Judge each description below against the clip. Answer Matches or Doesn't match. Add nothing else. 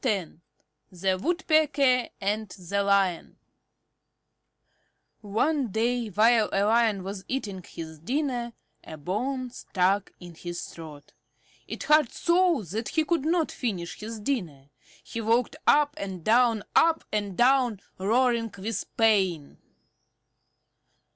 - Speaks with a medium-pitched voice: Doesn't match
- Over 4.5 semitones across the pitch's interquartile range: Matches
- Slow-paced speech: Matches